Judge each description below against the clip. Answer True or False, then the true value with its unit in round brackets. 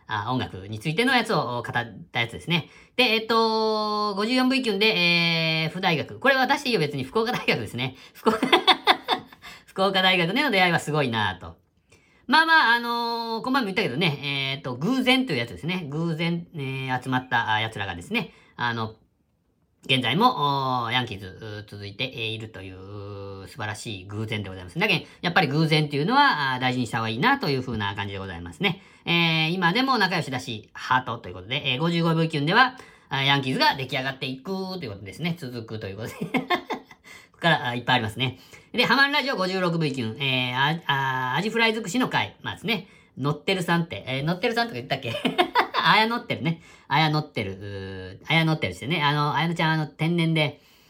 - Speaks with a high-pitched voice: False (145 Hz)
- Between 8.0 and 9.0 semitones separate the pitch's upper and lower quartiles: True (8.4 semitones)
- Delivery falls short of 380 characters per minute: False (400 characters per minute)